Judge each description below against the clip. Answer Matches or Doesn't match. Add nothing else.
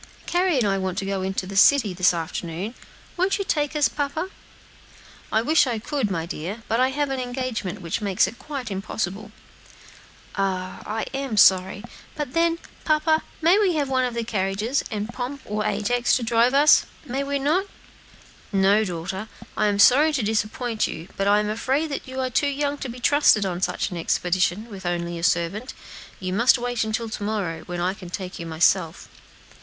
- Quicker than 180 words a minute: Matches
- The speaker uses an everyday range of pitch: Doesn't match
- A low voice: Doesn't match